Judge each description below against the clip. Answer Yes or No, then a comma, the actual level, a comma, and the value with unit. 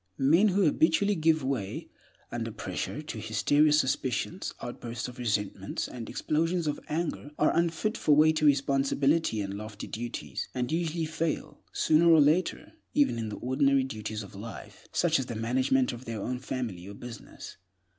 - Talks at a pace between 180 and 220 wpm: No, average, 160 wpm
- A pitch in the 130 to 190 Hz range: Yes, low, 135 Hz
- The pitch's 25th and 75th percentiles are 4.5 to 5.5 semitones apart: Yes, average, 5.2 semitones